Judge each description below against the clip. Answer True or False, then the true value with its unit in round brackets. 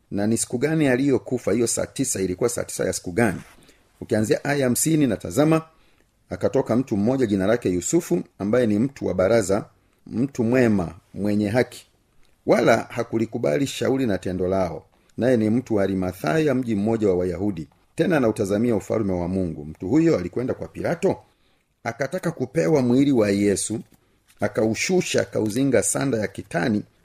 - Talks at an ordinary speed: False (155 wpm)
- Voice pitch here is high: False (115 Hz)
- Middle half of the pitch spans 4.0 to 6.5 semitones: True (5.0 semitones)